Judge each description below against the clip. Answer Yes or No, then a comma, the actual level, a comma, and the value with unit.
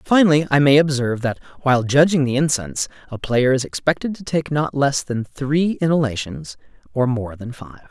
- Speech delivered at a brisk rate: No, average, 180 wpm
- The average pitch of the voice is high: No, low, 135 Hz